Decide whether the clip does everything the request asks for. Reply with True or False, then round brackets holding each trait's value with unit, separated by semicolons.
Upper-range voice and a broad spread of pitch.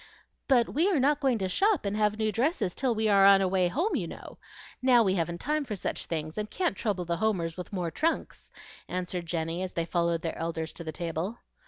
True (195 Hz; 6.0 semitones)